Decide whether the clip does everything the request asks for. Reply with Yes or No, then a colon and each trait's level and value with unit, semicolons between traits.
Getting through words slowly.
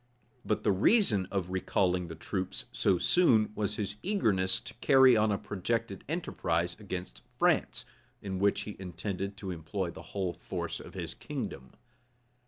No: average, 165 wpm